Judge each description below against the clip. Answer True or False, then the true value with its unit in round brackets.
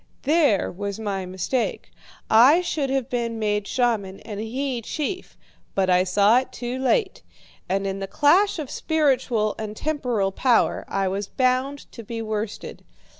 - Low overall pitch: False (230 Hz)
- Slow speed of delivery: False (155 wpm)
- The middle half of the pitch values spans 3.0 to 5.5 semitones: True (4.9 semitones)